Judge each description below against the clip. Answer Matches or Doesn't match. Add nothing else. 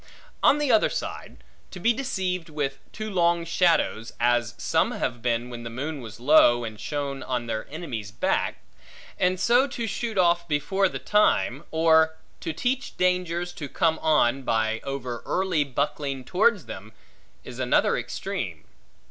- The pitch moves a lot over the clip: Matches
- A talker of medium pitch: Matches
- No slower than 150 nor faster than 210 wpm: Matches